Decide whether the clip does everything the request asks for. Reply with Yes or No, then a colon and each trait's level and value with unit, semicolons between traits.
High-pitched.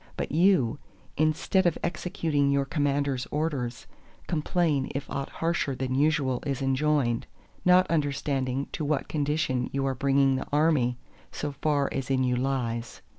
No: medium, 140 Hz